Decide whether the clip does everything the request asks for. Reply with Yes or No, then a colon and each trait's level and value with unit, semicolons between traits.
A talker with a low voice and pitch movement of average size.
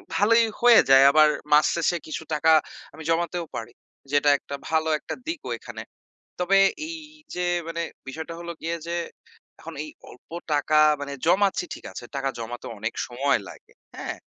No: medium, 160 Hz; average, 4.0 semitones